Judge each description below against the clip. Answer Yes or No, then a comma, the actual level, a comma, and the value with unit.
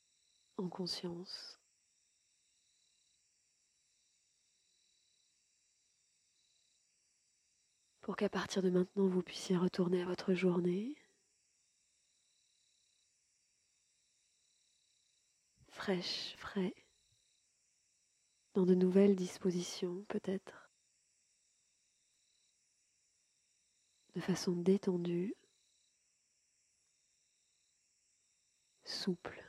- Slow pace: Yes, slow, 50 wpm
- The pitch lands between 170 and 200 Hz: Yes, medium, 185 Hz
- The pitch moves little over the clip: Yes, narrow, 1.5 semitones